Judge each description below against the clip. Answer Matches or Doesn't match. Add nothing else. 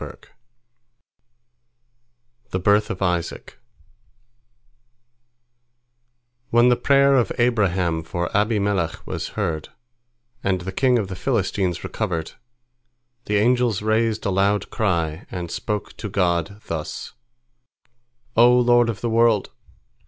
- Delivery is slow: Matches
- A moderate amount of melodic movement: Matches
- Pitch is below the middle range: Matches